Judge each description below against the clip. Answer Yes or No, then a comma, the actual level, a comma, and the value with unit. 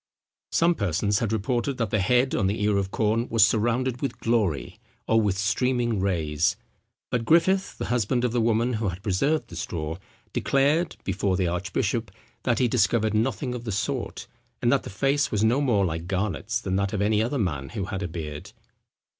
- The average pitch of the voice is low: Yes, low, 110 Hz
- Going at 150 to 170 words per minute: No, average, 195 wpm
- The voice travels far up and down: No, average, 4.2 semitones